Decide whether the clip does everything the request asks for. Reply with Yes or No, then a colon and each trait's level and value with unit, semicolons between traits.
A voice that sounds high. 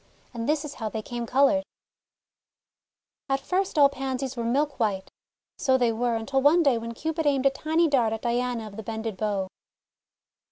Yes: very high, 255 Hz